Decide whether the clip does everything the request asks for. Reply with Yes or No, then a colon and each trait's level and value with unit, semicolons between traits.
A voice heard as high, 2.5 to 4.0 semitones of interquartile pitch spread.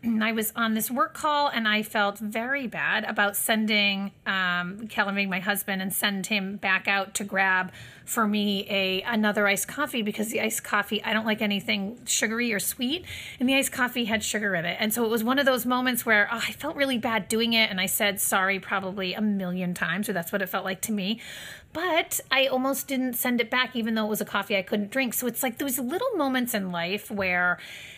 Yes: high, 215 Hz; average, 3.3 semitones